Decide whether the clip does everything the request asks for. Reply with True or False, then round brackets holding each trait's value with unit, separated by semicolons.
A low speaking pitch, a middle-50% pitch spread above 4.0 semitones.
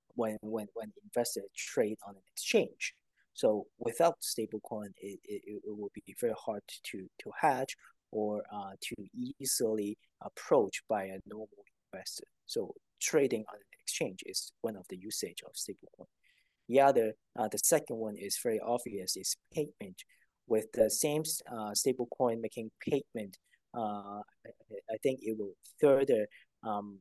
True (110 Hz; 4.6 semitones)